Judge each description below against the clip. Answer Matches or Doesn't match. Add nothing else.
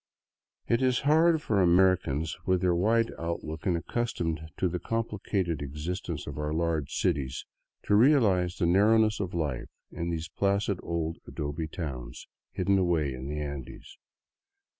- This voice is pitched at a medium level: Doesn't match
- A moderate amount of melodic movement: Matches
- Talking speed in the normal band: Matches